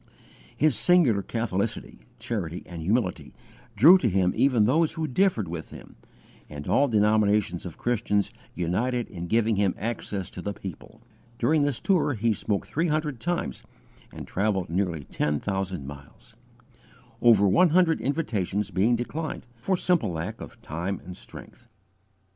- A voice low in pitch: Yes, low, 105 Hz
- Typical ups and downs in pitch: No, wide, 6.3 semitones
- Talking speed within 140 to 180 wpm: Yes, average, 150 wpm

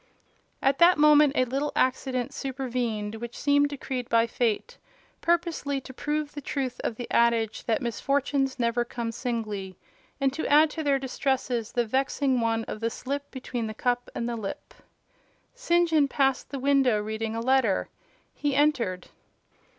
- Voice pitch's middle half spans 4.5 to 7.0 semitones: No, average, 3.5 semitones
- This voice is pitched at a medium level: No, very high, 260 Hz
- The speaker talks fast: No, average, 160 wpm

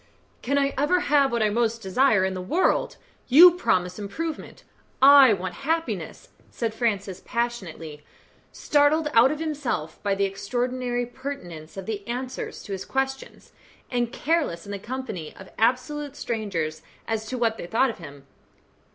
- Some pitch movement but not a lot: No, wide, 5.8 semitones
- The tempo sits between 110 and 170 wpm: Yes, average, 155 wpm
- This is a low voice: No, high, 235 Hz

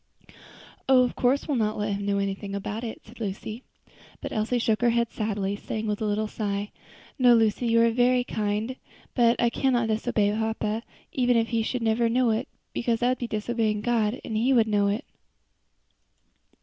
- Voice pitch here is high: Yes, high, 225 Hz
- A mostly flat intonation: Yes, narrow, 2.3 semitones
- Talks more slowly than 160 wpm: No, average, 190 wpm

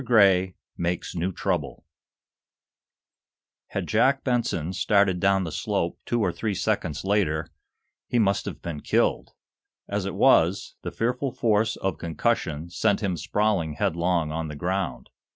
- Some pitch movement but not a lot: Yes, average, 4.0 semitones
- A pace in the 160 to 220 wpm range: No, average, 140 wpm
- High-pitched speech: No, very low, 95 Hz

